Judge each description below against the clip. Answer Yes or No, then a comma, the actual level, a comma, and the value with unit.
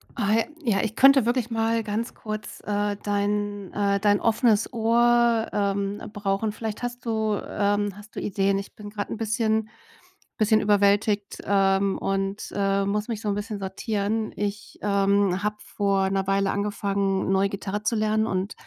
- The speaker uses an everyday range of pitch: No, narrow, 1.7 semitones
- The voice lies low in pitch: No, high, 205 Hz